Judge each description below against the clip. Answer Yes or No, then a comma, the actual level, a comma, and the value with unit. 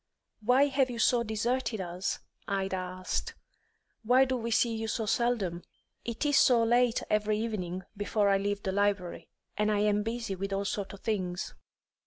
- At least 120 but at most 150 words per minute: No, average, 175 wpm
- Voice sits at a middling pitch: No, high, 210 Hz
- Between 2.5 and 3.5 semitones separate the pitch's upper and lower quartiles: Yes, average, 3.1 semitones